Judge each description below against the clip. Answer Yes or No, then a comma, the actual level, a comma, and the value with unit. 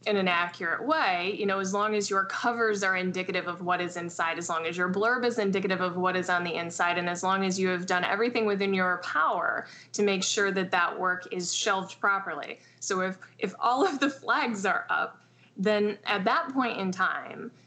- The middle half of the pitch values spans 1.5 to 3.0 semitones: Yes, average, 2.7 semitones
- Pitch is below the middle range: No, high, 190 Hz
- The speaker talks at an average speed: No, fast, 220 wpm